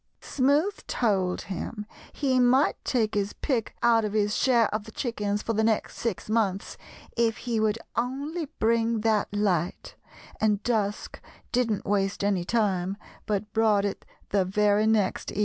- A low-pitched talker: No, high, 215 Hz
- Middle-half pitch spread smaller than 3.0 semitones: Yes, narrow, 2.4 semitones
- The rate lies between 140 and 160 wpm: Yes, average, 155 wpm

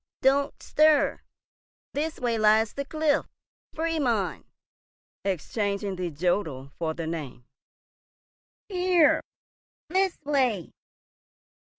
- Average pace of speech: No, slow, 85 wpm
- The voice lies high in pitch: Yes, high, 225 Hz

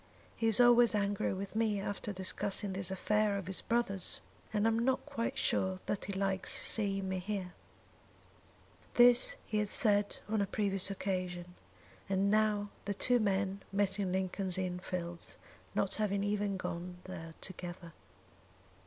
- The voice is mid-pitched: No, high, 200 Hz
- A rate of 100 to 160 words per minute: Yes, average, 155 wpm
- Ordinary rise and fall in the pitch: No, narrow, 2.0 semitones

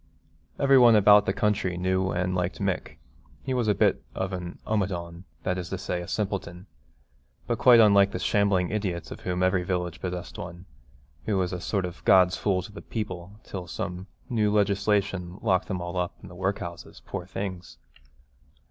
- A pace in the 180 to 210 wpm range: Yes, average, 185 wpm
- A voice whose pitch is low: Yes, very low, 95 Hz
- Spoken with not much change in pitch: Yes, narrow, 2.3 semitones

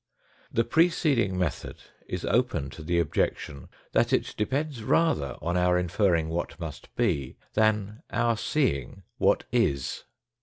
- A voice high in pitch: No, very low, 95 Hz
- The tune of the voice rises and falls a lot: Yes, wide, 6.4 semitones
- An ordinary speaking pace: No, slow, 130 wpm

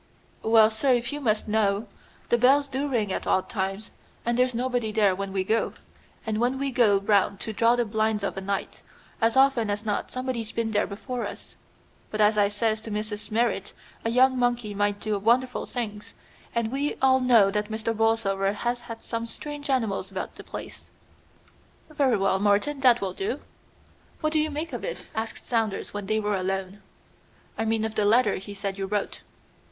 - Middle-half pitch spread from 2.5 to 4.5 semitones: Yes, average, 3.1 semitones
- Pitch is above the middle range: Yes, high, 220 Hz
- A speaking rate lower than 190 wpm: No, average, 195 wpm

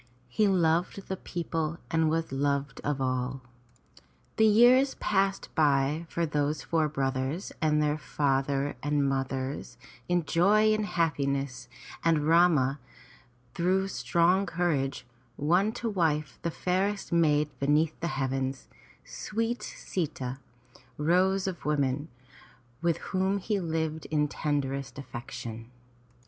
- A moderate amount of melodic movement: Yes, average, 4.4 semitones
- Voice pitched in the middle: Yes, medium, 155 Hz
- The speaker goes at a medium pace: No, slow, 120 wpm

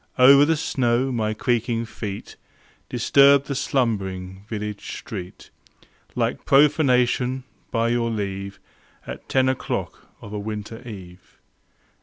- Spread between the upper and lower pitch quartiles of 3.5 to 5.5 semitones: Yes, average, 4.1 semitones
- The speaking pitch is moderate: No, low, 115 Hz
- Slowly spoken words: Yes, slow, 115 wpm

